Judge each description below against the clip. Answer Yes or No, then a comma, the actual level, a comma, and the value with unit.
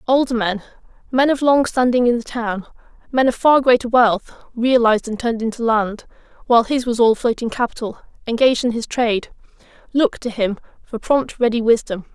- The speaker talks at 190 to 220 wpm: No, average, 170 wpm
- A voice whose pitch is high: Yes, high, 235 Hz